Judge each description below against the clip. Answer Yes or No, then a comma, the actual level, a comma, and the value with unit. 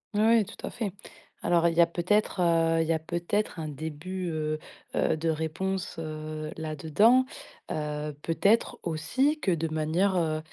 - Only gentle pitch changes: No, average, 3.3 semitones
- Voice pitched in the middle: Yes, medium, 165 Hz